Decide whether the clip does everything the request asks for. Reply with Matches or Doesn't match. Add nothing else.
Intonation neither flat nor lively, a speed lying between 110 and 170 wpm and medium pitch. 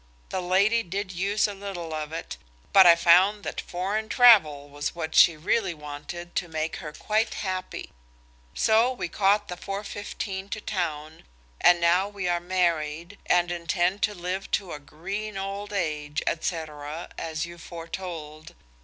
Matches